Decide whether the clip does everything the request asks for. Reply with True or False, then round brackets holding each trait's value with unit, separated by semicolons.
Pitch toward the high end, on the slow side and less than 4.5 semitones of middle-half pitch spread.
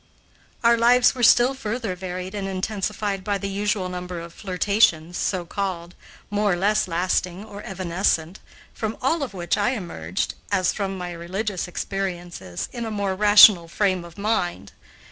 False (195 Hz; 160 wpm; 2.9 semitones)